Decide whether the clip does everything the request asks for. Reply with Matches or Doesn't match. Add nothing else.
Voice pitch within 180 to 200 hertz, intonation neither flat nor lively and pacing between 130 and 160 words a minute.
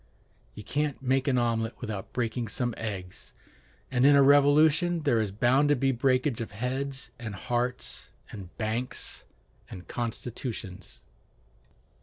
Doesn't match